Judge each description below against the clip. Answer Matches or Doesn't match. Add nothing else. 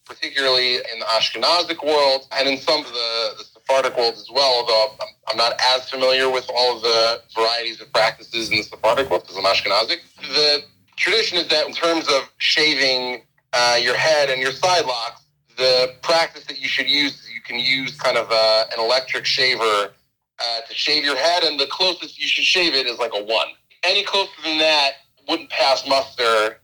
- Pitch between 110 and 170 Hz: Matches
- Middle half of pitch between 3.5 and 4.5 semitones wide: Matches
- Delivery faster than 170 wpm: Matches